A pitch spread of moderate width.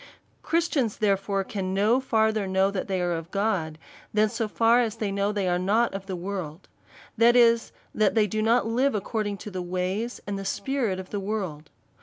Yes: average, 3.0 semitones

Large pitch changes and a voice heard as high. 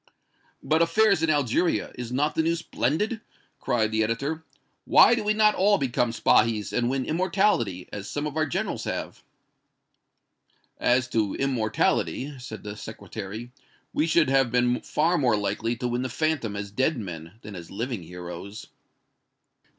No: wide, 6.4 semitones; low, 125 Hz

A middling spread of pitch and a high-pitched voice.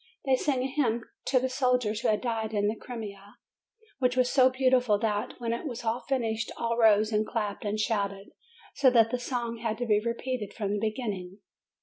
Yes: average, 3.0 semitones; high, 230 Hz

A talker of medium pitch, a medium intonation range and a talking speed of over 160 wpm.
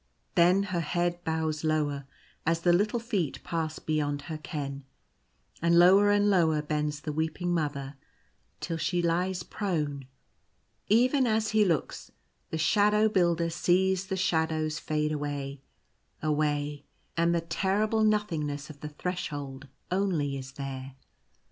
No: medium, 165 Hz; average, 4.0 semitones; slow, 135 wpm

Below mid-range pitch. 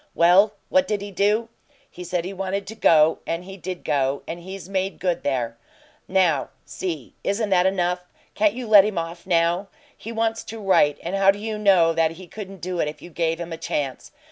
No: medium, 185 Hz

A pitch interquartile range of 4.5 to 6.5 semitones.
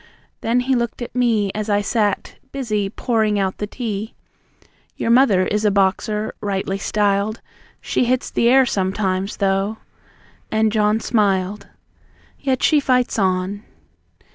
No: average, 3.1 semitones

